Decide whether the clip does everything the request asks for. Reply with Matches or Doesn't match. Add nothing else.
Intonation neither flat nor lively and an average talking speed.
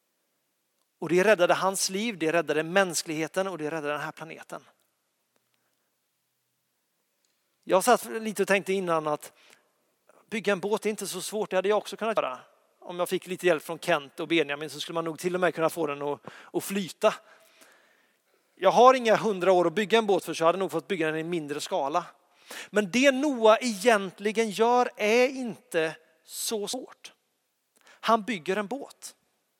Matches